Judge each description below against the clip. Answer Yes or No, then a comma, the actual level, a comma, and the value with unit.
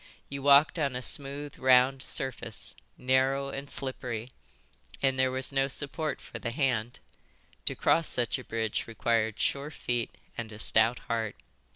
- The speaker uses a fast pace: No, average, 155 wpm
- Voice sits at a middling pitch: No, low, 130 Hz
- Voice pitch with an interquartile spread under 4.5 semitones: Yes, average, 2.9 semitones